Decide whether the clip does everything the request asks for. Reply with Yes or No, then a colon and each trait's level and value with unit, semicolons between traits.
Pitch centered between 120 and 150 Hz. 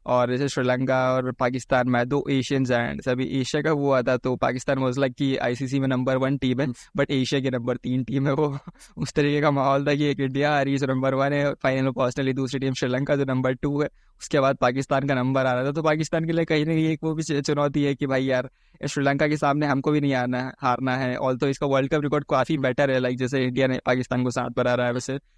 Yes: low, 135 Hz